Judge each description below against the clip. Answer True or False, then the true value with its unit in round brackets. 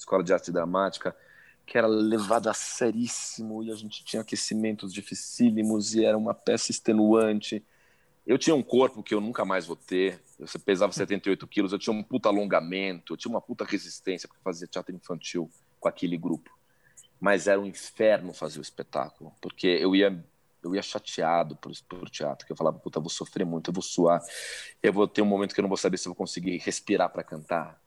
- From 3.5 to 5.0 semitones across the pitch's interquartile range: False (2.8 semitones)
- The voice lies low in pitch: True (100 Hz)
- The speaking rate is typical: False (205 wpm)